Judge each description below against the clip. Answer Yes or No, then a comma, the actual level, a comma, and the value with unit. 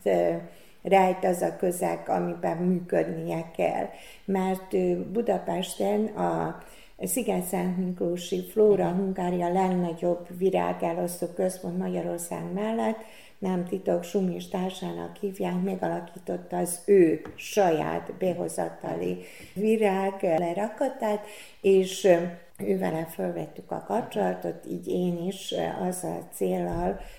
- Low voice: No, medium, 185 Hz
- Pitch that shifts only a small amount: Yes, narrow, 2.1 semitones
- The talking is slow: Yes, slow, 95 wpm